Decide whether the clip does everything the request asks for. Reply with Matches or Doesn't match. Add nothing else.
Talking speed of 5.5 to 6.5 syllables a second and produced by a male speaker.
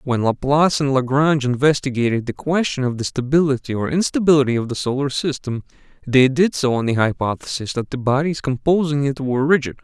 Matches